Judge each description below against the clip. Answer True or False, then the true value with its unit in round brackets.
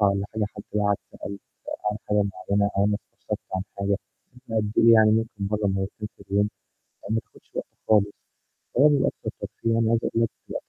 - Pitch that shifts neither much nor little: False (1.9 semitones)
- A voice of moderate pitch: False (105 Hz)